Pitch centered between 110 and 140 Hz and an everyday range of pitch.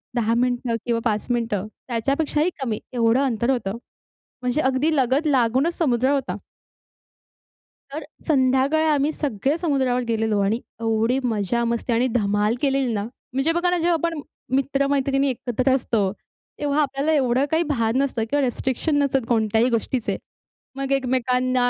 No: very high, 255 Hz; average, 3.3 semitones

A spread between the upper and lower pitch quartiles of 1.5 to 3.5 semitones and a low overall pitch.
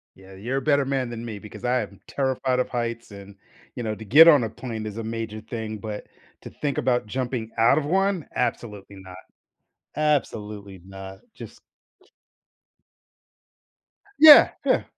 No: average, 3.9 semitones; low, 115 Hz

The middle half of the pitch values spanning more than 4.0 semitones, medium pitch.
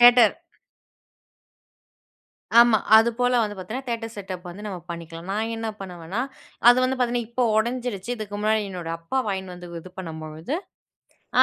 No: average, 4.8 semitones; high, 210 Hz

